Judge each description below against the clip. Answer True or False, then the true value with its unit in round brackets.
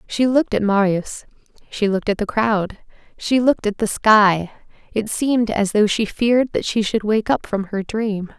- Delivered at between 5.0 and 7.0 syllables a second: False (4.8 syllables/s)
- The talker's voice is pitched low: False (215 Hz)